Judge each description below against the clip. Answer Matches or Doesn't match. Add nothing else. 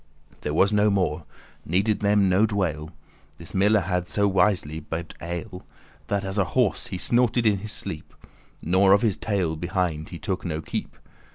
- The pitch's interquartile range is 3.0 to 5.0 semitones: Matches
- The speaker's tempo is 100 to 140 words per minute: Doesn't match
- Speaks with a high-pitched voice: Doesn't match